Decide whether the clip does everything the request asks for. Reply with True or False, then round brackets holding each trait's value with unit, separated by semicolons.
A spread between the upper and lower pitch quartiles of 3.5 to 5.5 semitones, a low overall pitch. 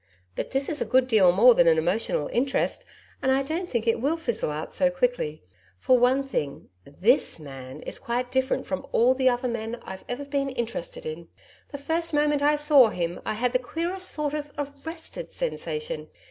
False (4.7 semitones; 260 Hz)